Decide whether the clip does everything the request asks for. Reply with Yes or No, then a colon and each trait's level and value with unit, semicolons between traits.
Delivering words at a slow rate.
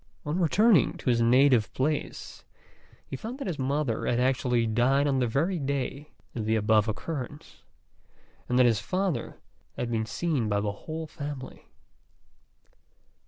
No: average, 150 wpm